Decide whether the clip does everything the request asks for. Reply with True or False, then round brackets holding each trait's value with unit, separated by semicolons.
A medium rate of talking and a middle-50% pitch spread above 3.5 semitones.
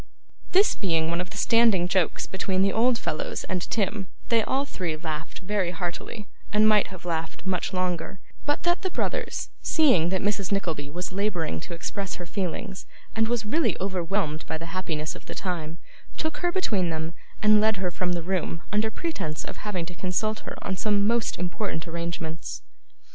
True (185 wpm; 3.9 semitones)